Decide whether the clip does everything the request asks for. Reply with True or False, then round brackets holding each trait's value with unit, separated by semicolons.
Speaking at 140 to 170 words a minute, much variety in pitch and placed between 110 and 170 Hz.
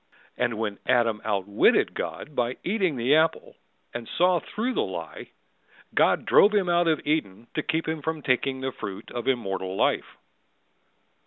True (160 wpm; 6.3 semitones; 135 Hz)